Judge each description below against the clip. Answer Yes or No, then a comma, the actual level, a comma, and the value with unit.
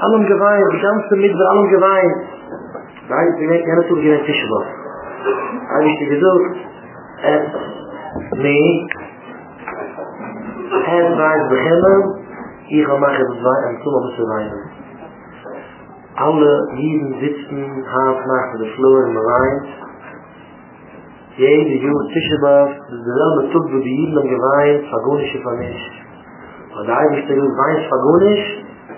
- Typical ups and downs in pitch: Yes, average, 4.4 semitones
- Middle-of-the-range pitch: Yes, medium, 145 Hz